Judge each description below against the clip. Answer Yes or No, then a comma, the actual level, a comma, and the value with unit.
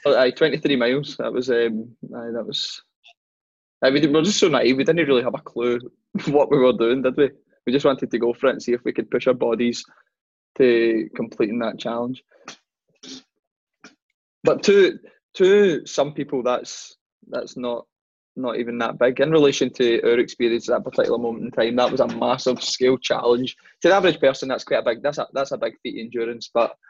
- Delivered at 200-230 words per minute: Yes, fast, 205 wpm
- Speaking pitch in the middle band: No, low, 125 Hz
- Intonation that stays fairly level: No, average, 3.2 semitones